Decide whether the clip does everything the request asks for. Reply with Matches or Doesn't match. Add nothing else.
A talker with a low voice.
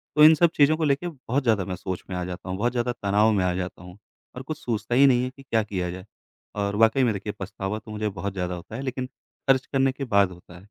Matches